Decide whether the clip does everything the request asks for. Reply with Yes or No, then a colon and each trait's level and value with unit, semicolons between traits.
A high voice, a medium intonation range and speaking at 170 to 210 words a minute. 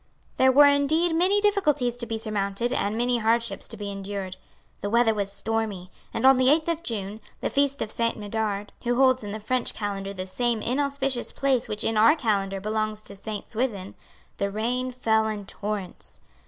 Yes: high, 225 Hz; average, 4.1 semitones; average, 190 wpm